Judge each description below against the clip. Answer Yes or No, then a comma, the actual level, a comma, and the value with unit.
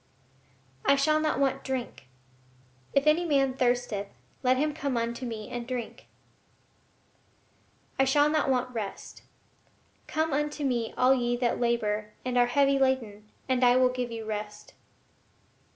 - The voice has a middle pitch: No, very high, 255 Hz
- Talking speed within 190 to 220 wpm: No, average, 145 wpm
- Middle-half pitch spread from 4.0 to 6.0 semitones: No, average, 2.7 semitones